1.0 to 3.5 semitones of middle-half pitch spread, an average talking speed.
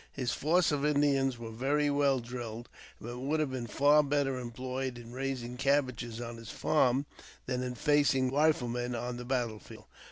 Yes: average, 2.9 semitones; average, 180 wpm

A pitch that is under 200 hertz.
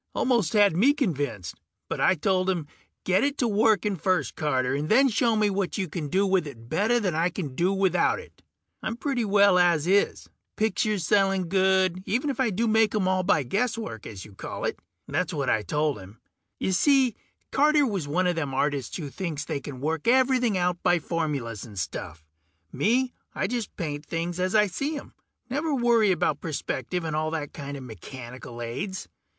Yes: medium, 185 Hz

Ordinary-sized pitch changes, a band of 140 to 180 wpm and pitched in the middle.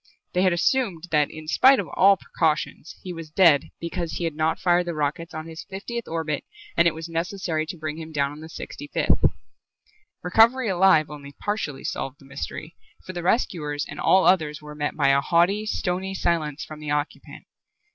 No: average, 3.3 semitones; average, 195 wpm; medium, 165 Hz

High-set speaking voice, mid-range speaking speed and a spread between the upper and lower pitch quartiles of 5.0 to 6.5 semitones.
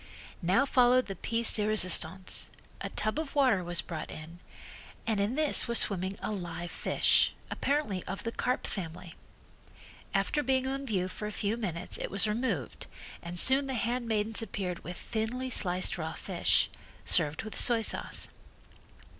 Yes: high, 210 Hz; average, 160 wpm; wide, 5.4 semitones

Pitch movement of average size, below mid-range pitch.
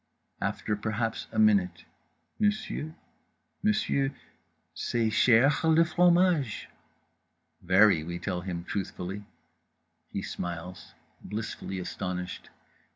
No: wide, 6.9 semitones; low, 105 Hz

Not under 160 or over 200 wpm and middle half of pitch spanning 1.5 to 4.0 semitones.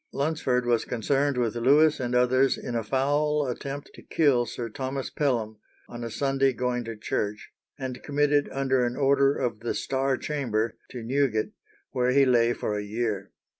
Yes: average, 170 wpm; average, 2.8 semitones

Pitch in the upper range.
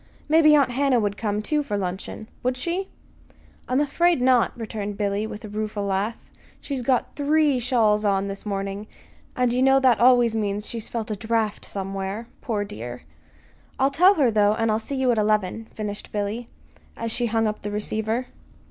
Yes: high, 225 Hz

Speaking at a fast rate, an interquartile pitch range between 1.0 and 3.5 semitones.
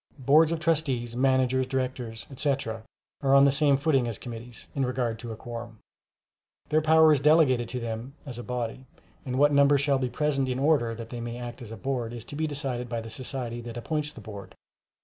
Yes: fast, 210 wpm; average, 3.1 semitones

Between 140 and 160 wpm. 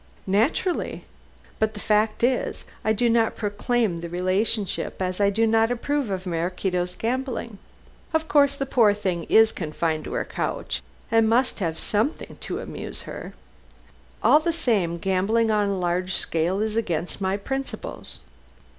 Yes: average, 155 wpm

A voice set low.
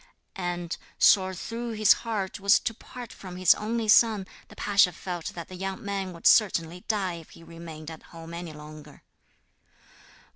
No: medium, 185 Hz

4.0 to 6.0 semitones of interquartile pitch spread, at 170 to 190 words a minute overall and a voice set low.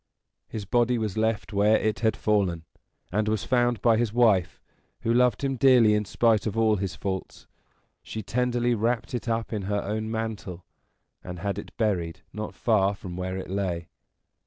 No: average, 2.9 semitones; average, 180 wpm; low, 110 Hz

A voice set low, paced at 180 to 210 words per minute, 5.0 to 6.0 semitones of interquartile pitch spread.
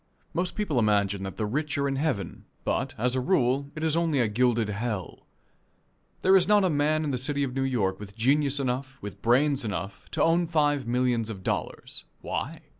Yes: low, 130 Hz; average, 200 wpm; average, 5.3 semitones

